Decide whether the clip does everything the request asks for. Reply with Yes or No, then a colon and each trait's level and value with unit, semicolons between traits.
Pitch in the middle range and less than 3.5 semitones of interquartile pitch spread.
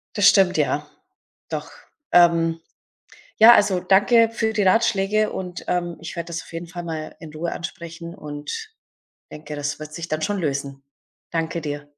No: medium, 170 Hz; average, 3.8 semitones